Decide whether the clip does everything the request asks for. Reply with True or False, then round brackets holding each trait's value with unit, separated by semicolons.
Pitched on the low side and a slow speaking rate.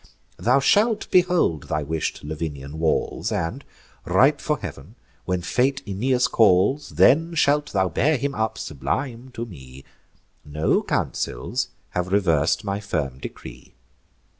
True (100 Hz; 130 wpm)